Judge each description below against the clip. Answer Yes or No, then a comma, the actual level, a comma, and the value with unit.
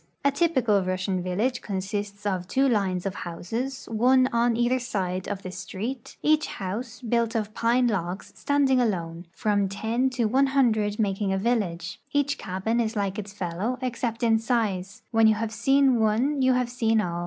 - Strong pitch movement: No, average, 4.3 semitones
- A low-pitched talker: No, high, 220 Hz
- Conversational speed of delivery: Yes, average, 180 wpm